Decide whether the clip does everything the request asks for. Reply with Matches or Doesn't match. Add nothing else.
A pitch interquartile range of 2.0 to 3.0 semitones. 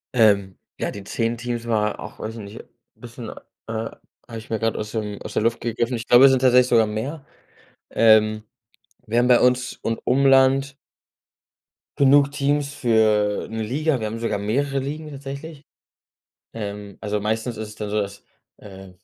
Doesn't match